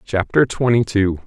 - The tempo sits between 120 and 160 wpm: Yes, average, 140 wpm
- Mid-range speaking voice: No, low, 110 Hz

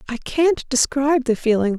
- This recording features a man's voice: No, female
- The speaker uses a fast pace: No, average, 170 wpm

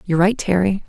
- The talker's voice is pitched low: No, high, 190 Hz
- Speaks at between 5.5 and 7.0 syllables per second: Yes, 6.5 syllables/s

